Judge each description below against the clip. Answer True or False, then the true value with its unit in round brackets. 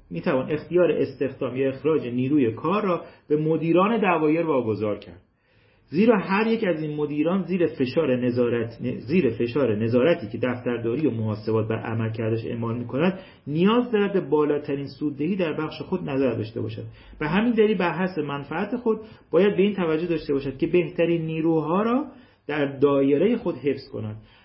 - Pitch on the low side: False (150 Hz)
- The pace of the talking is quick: True (165 wpm)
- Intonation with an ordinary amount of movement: False (6.4 semitones)